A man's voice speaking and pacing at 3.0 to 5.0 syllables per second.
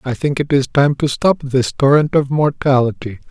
Yes: male; 4.9 syllables/s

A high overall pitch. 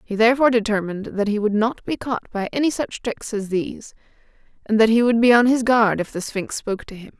Yes: high, 220 Hz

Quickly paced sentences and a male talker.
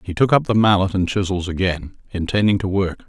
Yes: fast, 215 wpm; male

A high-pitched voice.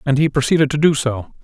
No: medium, 140 Hz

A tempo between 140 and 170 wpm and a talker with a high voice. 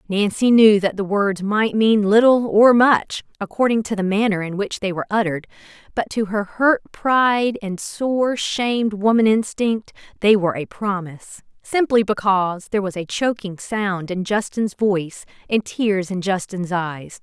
Yes: average, 165 wpm; high, 205 Hz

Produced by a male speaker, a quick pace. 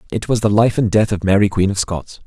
Yes: male; fast, 290 wpm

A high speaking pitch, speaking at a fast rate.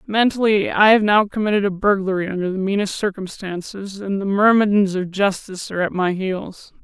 No: high, 195 Hz; average, 175 wpm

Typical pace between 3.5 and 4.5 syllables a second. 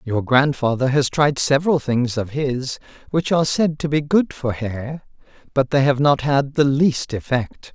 Yes: 4.4 syllables/s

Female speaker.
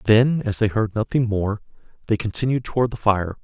No: male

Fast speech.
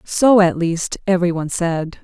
No: average, 175 wpm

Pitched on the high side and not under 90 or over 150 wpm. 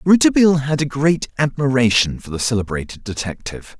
No: low, 130 Hz; average, 140 wpm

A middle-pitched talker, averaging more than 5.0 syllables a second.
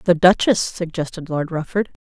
No: medium, 170 Hz; 4.7 syllables/s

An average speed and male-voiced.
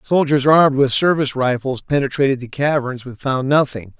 Yes: average, 165 wpm; male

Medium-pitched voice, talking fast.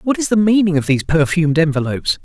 Yes: medium, 170 Hz; fast, 215 wpm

